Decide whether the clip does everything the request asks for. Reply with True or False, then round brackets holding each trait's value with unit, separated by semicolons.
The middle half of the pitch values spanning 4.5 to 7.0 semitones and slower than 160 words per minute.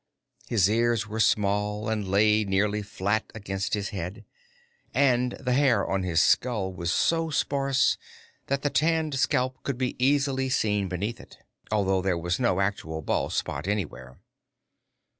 True (4.8 semitones; 150 wpm)